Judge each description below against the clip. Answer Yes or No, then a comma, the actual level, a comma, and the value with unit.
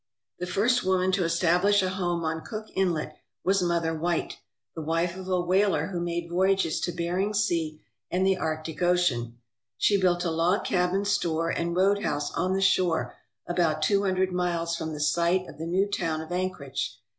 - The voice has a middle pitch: Yes, medium, 175 Hz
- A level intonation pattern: Yes, narrow, 2.2 semitones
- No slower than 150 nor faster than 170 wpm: No, average, 180 wpm